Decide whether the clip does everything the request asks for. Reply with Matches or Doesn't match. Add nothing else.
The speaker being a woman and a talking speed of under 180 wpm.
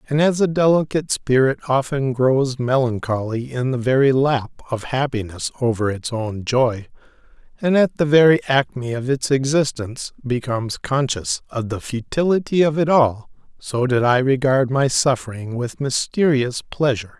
Doesn't match